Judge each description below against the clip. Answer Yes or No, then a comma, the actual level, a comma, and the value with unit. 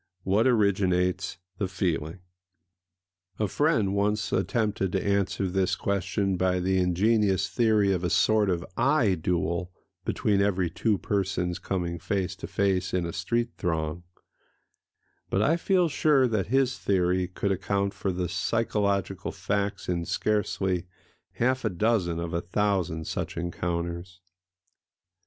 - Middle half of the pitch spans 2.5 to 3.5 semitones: Yes, average, 2.8 semitones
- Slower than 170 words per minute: Yes, slow, 135 wpm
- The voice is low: Yes, very low, 95 Hz